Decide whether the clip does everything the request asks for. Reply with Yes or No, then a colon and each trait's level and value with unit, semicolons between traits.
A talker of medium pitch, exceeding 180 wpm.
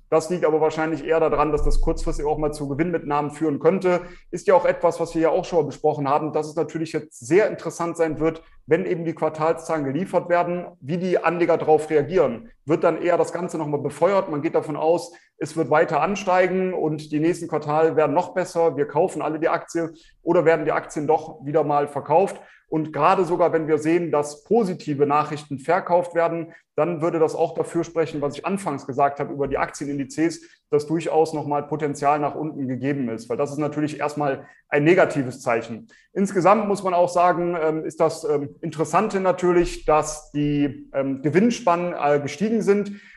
Yes: medium, 160 Hz; fast, 190 wpm